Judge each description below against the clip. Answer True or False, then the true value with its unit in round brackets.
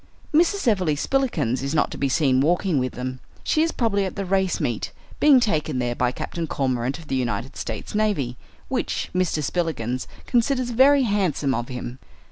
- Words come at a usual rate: True (180 wpm)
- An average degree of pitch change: False (8.7 semitones)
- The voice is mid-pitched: True (160 Hz)